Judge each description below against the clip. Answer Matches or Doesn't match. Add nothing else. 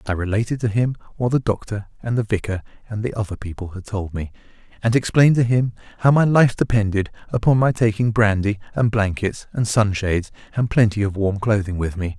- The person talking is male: Matches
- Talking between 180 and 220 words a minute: Matches